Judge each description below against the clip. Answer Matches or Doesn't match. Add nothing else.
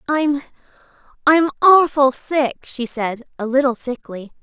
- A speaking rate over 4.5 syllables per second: Doesn't match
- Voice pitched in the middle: Doesn't match